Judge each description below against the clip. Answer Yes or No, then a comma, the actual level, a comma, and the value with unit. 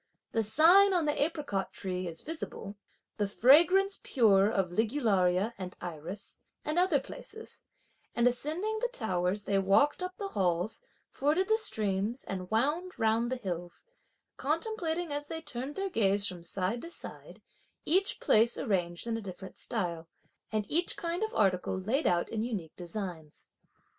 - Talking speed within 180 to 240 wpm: No, average, 160 wpm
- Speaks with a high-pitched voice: Yes, high, 225 Hz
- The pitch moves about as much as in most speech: No, wide, 8.9 semitones